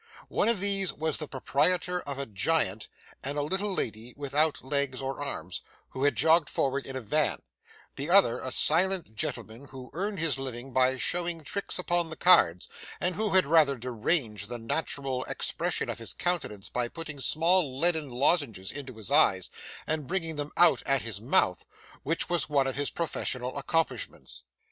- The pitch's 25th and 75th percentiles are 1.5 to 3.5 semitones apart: No, average, 4.6 semitones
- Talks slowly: No, average, 175 wpm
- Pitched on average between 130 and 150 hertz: Yes, medium, 140 Hz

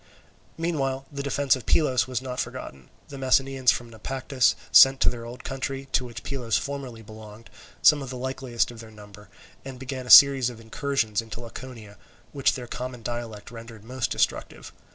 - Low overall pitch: Yes, low, 125 Hz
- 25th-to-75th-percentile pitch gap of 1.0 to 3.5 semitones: Yes, average, 2.9 semitones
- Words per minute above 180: No, average, 175 wpm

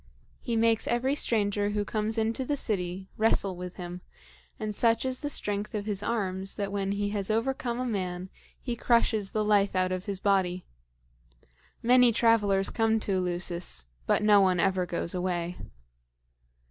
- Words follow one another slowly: No, average, 165 wpm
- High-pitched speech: Yes, high, 205 Hz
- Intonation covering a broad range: No, average, 3.3 semitones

